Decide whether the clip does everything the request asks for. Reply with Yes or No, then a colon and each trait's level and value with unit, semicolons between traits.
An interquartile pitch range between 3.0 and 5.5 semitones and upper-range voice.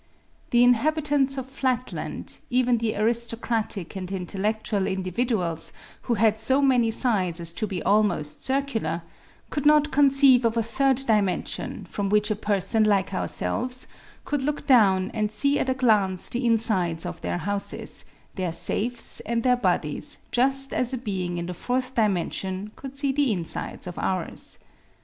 Yes: average, 5.1 semitones; high, 225 Hz